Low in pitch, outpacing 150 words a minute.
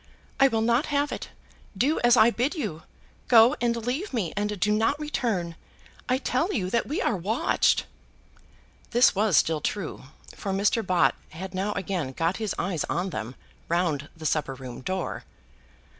No: high, 205 Hz; average, 170 wpm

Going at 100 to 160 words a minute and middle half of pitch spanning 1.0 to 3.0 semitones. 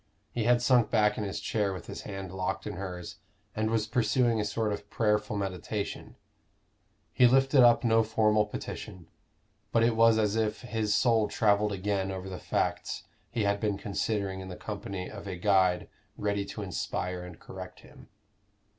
No: average, 175 wpm; narrow, 2.5 semitones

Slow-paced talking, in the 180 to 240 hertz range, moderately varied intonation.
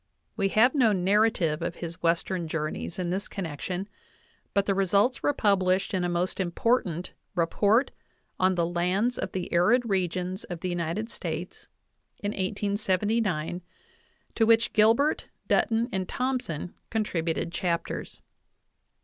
Yes: slow, 130 wpm; high, 190 Hz; average, 3.8 semitones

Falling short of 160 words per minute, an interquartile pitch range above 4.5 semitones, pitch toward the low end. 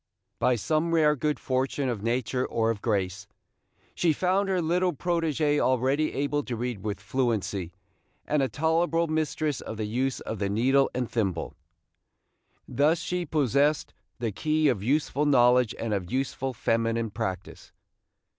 Yes: average, 150 wpm; average, 5.1 semitones; low, 130 Hz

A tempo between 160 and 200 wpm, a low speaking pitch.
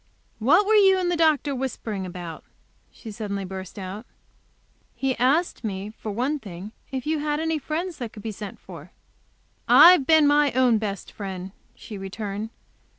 No: average, 165 wpm; high, 235 Hz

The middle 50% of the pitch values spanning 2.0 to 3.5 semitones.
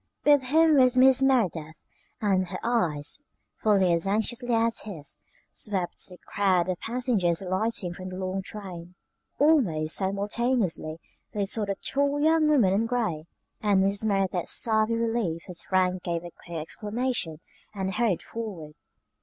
No: average, 4.8 semitones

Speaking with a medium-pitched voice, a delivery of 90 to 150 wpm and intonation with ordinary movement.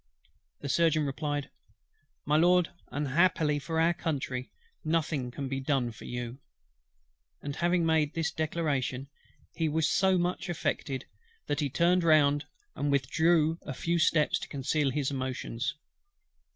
Yes: medium, 150 Hz; average, 140 wpm; average, 3.3 semitones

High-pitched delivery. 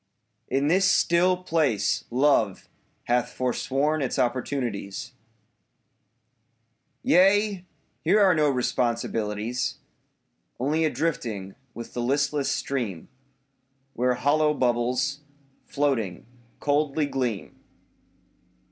No: low, 135 Hz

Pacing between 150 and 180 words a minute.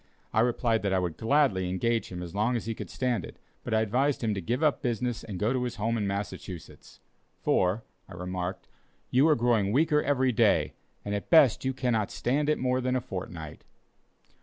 No: fast, 205 wpm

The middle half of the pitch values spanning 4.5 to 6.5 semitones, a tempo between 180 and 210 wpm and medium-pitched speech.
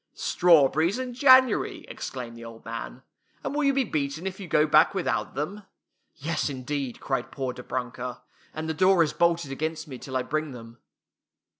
Yes: wide, 5.6 semitones; average, 190 wpm; medium, 150 Hz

